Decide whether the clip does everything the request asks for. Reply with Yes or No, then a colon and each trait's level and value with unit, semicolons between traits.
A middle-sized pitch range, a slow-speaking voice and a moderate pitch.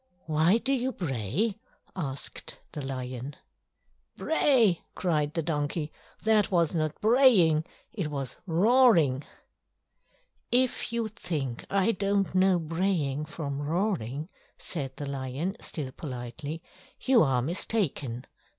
No: wide, 6.1 semitones; slow, 110 wpm; medium, 160 Hz